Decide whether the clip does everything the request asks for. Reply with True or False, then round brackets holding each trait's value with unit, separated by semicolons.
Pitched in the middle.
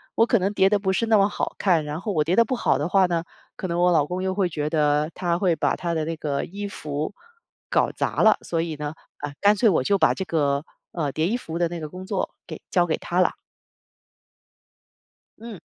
True (175 Hz)